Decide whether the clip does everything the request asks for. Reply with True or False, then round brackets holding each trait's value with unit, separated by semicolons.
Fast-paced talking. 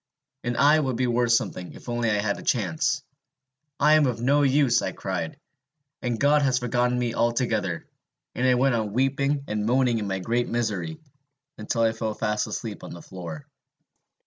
False (185 wpm)